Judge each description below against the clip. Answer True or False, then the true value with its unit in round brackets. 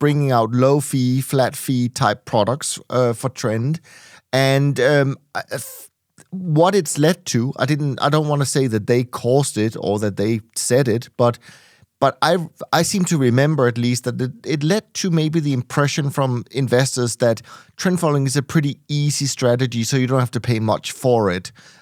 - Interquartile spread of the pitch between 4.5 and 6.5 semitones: False (3.4 semitones)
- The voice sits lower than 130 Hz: False (135 Hz)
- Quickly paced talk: False (185 wpm)